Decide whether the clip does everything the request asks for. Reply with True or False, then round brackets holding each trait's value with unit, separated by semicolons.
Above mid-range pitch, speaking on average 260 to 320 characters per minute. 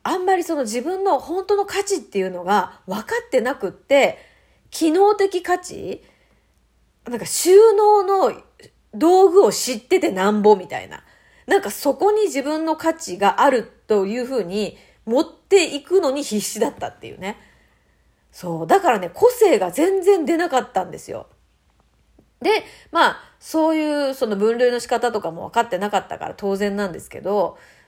True (305 Hz; 310 characters per minute)